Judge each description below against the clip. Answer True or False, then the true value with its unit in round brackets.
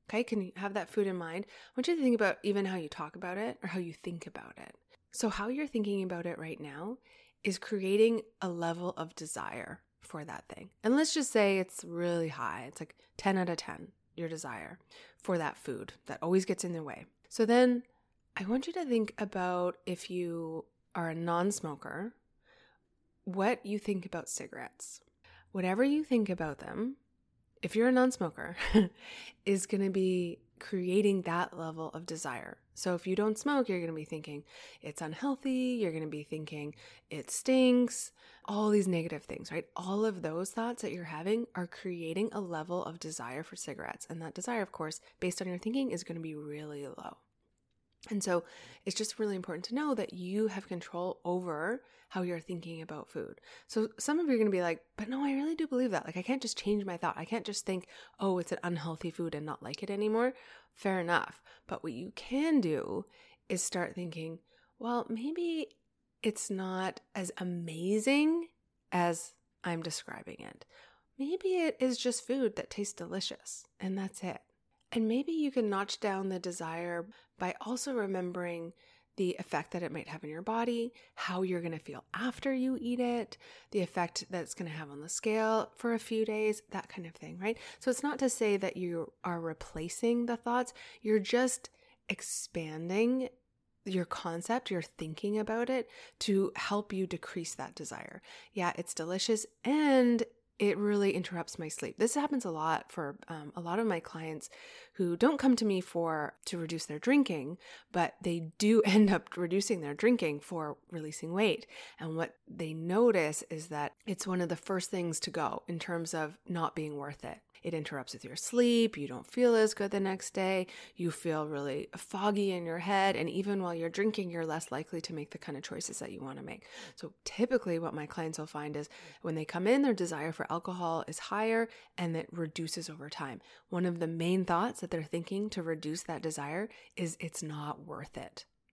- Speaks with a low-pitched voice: False (185 Hz)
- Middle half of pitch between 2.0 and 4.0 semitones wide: False (5.0 semitones)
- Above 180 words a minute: True (200 wpm)